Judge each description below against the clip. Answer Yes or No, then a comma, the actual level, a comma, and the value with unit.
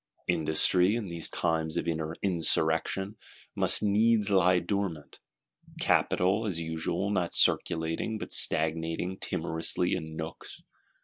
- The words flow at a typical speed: No, slow, 110 wpm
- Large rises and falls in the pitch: No, average, 3.3 semitones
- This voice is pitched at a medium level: No, very low, 85 Hz